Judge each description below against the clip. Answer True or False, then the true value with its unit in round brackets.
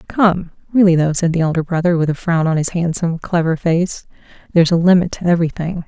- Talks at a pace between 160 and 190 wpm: False (205 wpm)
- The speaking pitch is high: False (170 Hz)